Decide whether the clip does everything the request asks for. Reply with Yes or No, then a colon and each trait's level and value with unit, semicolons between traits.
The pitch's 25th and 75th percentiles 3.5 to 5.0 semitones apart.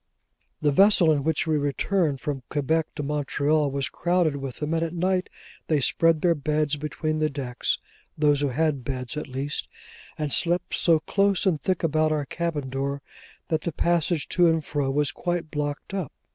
No: narrow, 2.6 semitones